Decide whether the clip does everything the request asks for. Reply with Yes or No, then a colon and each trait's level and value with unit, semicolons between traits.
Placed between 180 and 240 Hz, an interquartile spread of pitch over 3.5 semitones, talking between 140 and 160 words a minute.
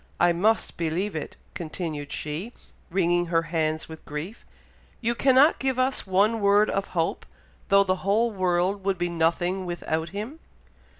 Yes: medium, 185 Hz; average, 3.9 semitones; average, 155 wpm